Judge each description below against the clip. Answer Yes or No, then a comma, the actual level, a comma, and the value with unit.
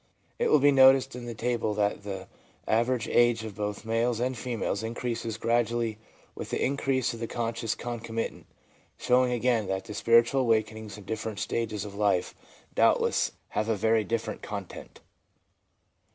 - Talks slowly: No, average, 150 wpm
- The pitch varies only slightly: Yes, narrow, 2.0 semitones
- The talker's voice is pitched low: Yes, low, 115 Hz